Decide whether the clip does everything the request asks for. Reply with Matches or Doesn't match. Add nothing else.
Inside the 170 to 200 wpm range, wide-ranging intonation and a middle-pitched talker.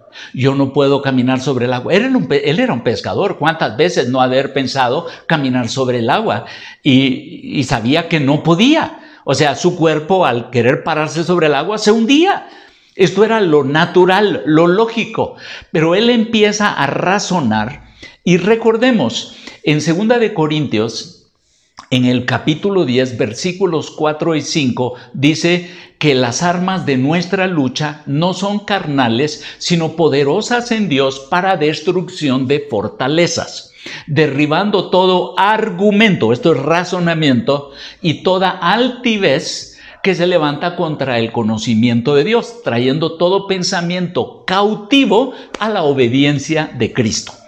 Doesn't match